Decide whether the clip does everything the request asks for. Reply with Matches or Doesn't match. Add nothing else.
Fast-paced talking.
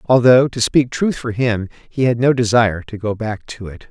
Matches